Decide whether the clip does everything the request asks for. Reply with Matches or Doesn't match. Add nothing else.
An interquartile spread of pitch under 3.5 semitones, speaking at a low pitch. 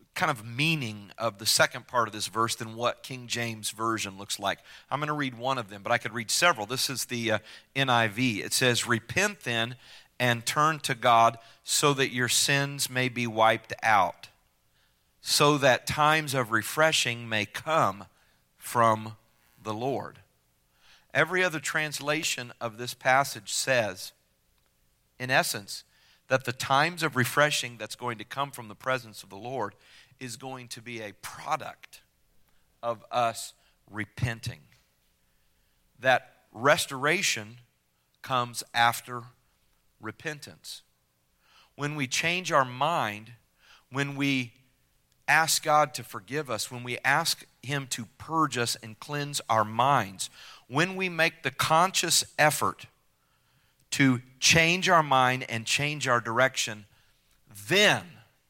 Doesn't match